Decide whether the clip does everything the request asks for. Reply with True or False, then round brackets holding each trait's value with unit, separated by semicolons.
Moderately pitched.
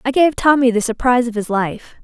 False (245 Hz)